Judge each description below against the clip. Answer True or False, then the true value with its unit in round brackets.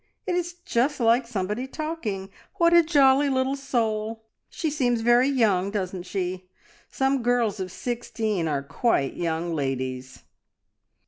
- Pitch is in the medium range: False (230 Hz)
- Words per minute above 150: False (135 wpm)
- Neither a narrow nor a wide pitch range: False (6.3 semitones)